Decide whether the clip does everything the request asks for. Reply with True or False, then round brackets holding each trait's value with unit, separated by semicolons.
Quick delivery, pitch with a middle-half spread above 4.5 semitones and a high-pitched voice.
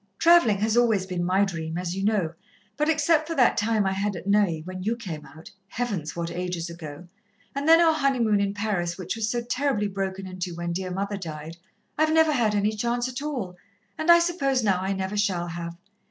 True (210 wpm; 5.3 semitones; 200 Hz)